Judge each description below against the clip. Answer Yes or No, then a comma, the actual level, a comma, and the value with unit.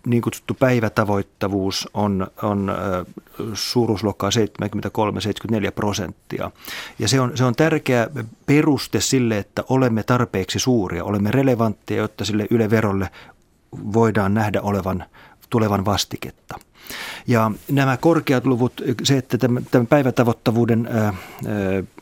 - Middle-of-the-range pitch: No, low, 110 Hz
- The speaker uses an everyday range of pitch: Yes, average, 3.6 semitones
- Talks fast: No, average, 110 wpm